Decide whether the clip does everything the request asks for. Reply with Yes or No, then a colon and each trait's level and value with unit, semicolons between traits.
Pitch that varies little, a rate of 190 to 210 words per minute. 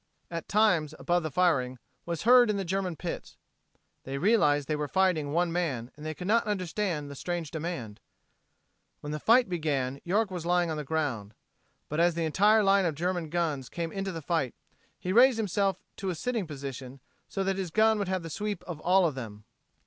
No: average, 4.5 semitones; average, 200 wpm